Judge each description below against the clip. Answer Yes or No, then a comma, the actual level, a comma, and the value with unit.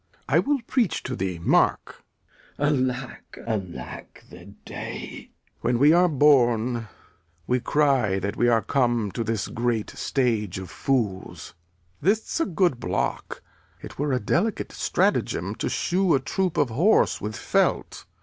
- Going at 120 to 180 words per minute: Yes, average, 150 wpm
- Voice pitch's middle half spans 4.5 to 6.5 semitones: Yes, average, 5.2 semitones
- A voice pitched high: No, low, 125 Hz